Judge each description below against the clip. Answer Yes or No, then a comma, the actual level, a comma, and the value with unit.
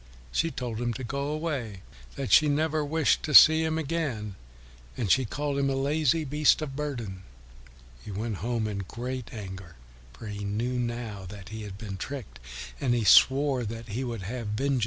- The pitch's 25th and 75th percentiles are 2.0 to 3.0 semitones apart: No, average, 5.3 semitones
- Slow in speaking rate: No, average, 195 wpm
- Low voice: Yes, low, 120 Hz